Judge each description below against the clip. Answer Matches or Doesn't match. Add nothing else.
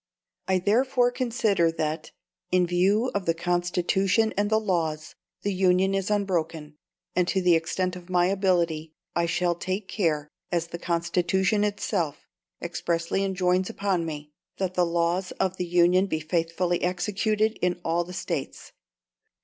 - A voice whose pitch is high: Doesn't match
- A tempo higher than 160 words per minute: Doesn't match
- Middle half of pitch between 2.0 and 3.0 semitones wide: Matches